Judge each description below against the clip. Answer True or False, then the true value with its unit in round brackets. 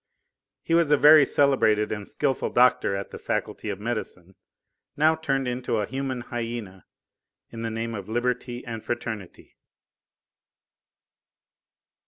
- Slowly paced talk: True (130 wpm)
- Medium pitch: False (120 Hz)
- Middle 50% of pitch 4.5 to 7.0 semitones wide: False (3.9 semitones)